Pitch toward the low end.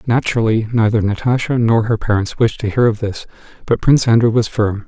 Yes: low, 115 Hz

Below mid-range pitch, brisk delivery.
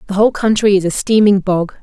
No: high, 200 Hz; fast, 230 wpm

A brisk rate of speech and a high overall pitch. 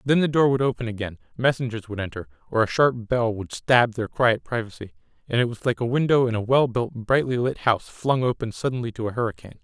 No: fast, 230 wpm; low, 120 Hz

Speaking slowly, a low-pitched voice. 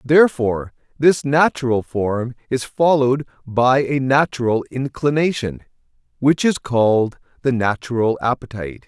Yes: slow, 110 wpm; low, 125 Hz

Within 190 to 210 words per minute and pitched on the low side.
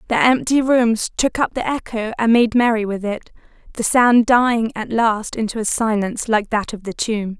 No: fast, 205 wpm; high, 225 Hz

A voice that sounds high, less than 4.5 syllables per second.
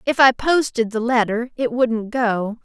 Yes: high, 235 Hz; 4.1 syllables/s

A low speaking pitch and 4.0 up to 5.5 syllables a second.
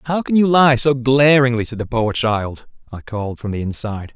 Yes: low, 125 Hz; 5.3 syllables/s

